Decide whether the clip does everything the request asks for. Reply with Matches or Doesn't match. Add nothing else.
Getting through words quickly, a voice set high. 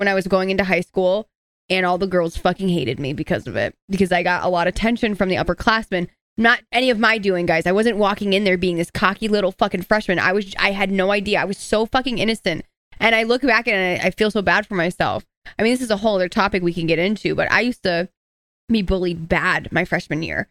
Matches